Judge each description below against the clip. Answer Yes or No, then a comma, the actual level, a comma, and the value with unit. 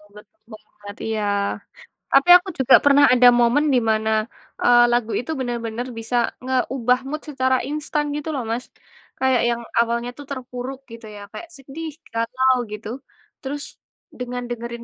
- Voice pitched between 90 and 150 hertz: No, very high, 250 Hz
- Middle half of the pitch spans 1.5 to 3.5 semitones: Yes, narrow, 2.6 semitones